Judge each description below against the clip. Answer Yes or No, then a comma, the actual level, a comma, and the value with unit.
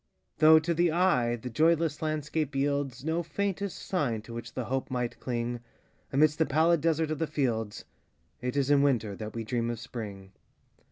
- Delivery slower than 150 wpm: No, average, 165 wpm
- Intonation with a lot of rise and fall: No, average, 5.0 semitones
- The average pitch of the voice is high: No, medium, 140 Hz